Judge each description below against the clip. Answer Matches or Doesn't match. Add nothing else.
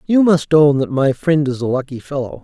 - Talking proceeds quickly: Matches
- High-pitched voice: Doesn't match